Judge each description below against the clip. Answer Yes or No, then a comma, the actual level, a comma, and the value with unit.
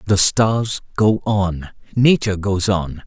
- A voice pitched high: No, low, 100 Hz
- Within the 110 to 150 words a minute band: Yes, slow, 135 wpm